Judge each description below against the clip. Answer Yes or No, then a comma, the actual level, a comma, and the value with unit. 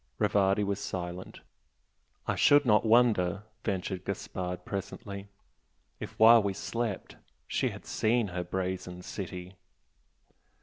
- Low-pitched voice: Yes, low, 100 Hz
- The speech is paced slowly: Yes, slow, 115 wpm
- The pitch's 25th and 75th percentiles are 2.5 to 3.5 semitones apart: Yes, average, 2.8 semitones